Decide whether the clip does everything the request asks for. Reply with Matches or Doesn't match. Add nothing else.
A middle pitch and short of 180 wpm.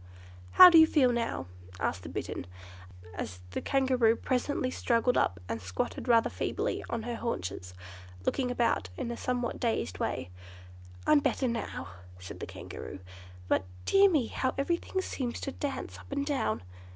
Doesn't match